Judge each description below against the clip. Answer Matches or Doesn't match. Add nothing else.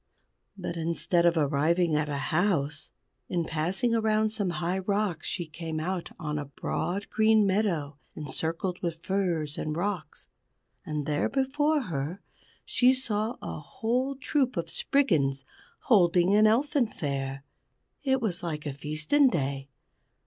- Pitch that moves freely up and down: Matches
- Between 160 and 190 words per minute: Doesn't match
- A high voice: Doesn't match